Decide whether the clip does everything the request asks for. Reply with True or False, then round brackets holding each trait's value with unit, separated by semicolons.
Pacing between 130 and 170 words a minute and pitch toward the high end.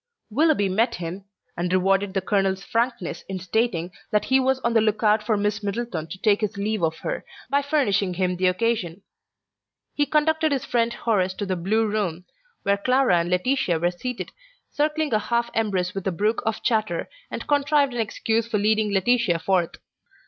False (185 wpm; 210 Hz)